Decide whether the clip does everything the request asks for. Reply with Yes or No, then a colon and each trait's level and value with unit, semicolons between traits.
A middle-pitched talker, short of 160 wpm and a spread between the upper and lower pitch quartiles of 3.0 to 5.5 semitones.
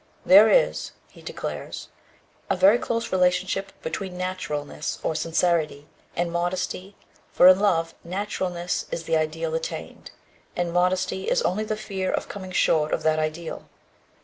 No: medium, 180 Hz; average, 145 wpm; narrow, 2.5 semitones